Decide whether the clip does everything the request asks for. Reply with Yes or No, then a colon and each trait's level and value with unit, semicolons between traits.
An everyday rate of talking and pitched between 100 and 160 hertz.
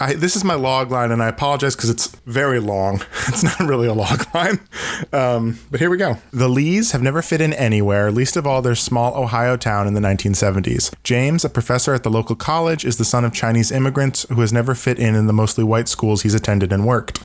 No: fast, 235 wpm; low, 125 Hz